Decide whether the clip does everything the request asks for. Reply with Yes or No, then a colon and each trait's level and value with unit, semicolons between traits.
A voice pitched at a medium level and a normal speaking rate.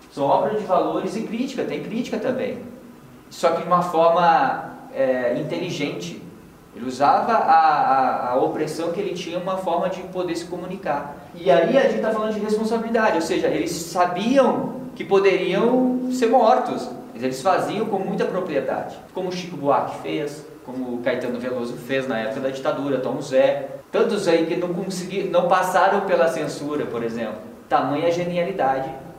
Yes: medium, 180 Hz; average, 165 wpm